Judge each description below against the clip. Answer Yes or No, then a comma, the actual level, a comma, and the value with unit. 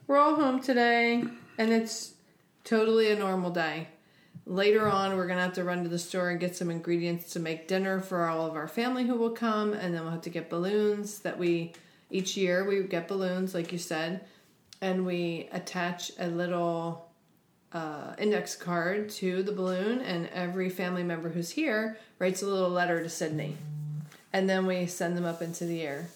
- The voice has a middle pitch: Yes, medium, 180 Hz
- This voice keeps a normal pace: Yes, average, 195 wpm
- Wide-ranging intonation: No, average, 2.7 semitones